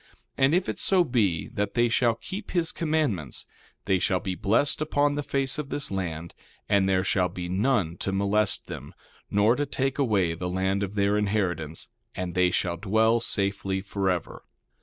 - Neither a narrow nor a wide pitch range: No, wide, 5.7 semitones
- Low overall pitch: Yes, low, 100 Hz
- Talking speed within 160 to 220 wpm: Yes, average, 180 wpm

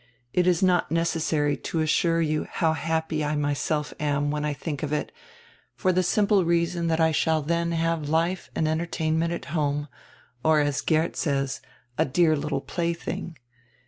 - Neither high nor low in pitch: Yes, medium, 160 Hz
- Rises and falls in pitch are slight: Yes, narrow, 2.1 semitones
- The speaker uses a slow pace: No, average, 170 wpm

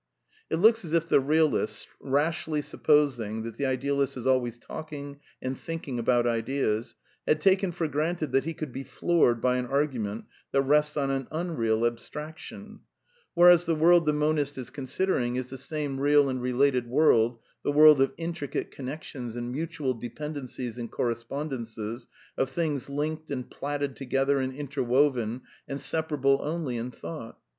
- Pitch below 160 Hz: Yes, medium, 140 Hz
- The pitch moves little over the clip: No, average, 3.6 semitones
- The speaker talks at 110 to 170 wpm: Yes, average, 160 wpm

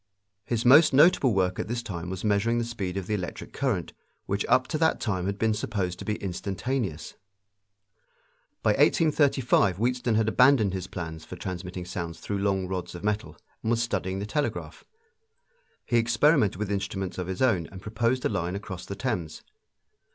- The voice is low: Yes, low, 105 Hz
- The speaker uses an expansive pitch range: No, average, 4.3 semitones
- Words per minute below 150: No, average, 180 wpm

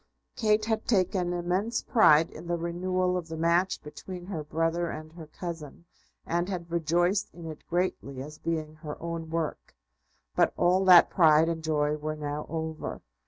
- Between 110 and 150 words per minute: No, average, 165 wpm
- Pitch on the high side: No, medium, 170 Hz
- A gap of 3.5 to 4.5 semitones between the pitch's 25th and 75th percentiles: No, narrow, 2.5 semitones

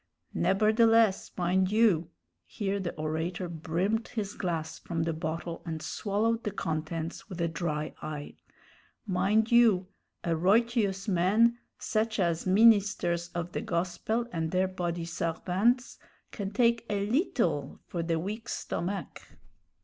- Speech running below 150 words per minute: Yes, slow, 135 wpm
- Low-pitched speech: No, medium, 185 Hz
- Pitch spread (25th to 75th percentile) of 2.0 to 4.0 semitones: No, average, 4.4 semitones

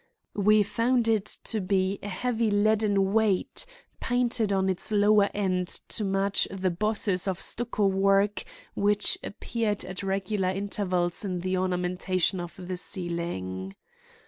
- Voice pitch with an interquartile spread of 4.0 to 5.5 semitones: No, narrow, 2.4 semitones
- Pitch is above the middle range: Yes, high, 195 Hz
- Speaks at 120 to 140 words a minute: Yes, slow, 135 wpm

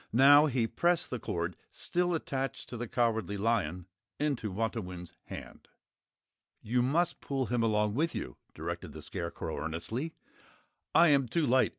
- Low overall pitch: Yes, low, 120 Hz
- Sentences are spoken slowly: No, average, 150 wpm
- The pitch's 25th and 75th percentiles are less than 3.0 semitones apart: No, average, 5.2 semitones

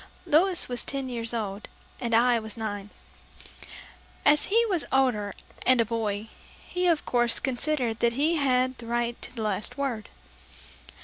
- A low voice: No, high, 240 Hz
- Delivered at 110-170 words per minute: Yes, average, 160 wpm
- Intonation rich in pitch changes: No, average, 3.8 semitones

